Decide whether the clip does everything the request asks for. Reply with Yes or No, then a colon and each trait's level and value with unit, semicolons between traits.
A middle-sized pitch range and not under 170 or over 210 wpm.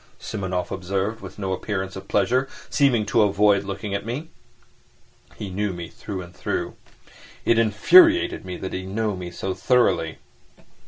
No: average, 3.0 semitones; average, 155 wpm